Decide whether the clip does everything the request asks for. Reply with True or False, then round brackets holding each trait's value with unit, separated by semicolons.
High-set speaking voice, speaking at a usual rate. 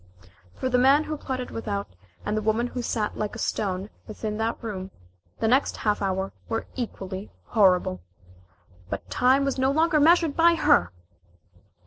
True (225 Hz; 160 wpm)